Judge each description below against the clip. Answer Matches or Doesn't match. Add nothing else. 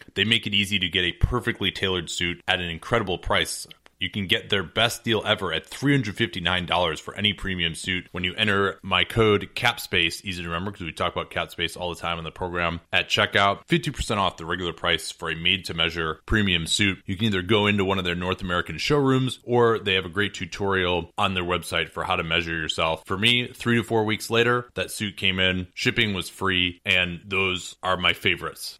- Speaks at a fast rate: Matches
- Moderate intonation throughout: Matches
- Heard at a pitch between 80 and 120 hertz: Matches